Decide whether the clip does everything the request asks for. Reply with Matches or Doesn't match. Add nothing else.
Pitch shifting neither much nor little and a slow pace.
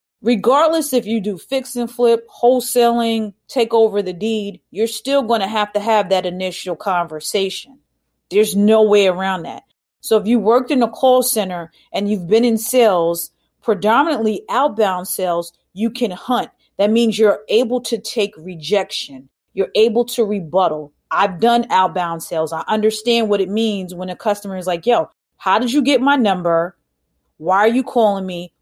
Doesn't match